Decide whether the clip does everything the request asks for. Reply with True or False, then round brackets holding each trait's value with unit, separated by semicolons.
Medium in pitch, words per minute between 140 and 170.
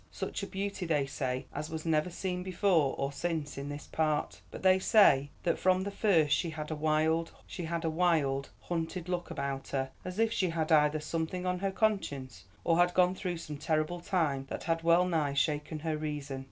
False (160 Hz; 195 wpm)